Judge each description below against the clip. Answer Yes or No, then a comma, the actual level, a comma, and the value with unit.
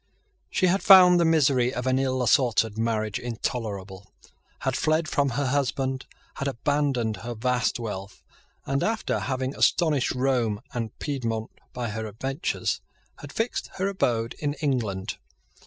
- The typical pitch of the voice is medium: No, low, 130 Hz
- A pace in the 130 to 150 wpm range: Yes, average, 140 wpm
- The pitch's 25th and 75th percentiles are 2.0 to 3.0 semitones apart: No, average, 4.0 semitones